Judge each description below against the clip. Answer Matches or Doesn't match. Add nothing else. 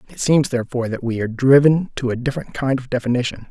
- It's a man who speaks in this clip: Matches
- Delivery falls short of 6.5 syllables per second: Doesn't match